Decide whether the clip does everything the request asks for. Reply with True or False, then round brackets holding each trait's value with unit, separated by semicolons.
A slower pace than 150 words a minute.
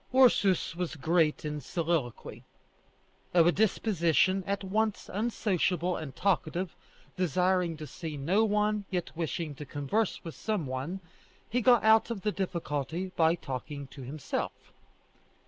True (135 wpm)